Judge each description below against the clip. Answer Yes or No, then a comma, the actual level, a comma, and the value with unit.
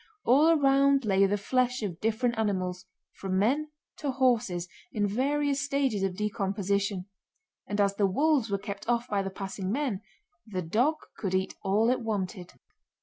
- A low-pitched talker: No, high, 210 Hz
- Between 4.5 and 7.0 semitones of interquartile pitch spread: Yes, average, 4.9 semitones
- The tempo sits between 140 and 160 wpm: Yes, average, 150 wpm